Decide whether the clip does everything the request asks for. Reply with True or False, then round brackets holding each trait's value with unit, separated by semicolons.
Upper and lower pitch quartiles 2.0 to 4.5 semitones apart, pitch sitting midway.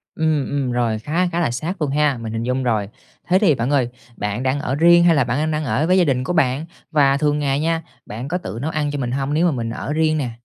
True (4.0 semitones; 145 Hz)